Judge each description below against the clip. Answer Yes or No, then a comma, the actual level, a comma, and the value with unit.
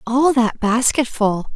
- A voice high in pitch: Yes, high, 240 Hz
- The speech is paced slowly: Yes, slow, 115 wpm